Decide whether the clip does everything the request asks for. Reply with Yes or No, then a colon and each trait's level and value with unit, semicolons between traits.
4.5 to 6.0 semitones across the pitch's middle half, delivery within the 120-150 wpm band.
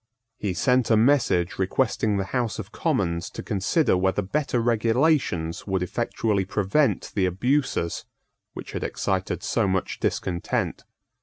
Yes: average, 5.2 semitones; slow, 135 wpm